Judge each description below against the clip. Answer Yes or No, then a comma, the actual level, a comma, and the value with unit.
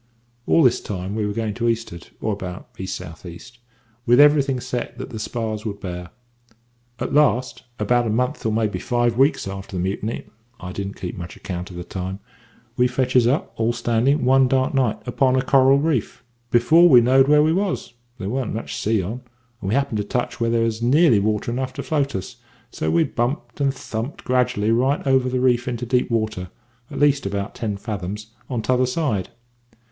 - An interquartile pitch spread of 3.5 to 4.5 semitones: Yes, average, 3.9 semitones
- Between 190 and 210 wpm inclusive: Yes, average, 200 wpm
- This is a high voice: No, low, 120 Hz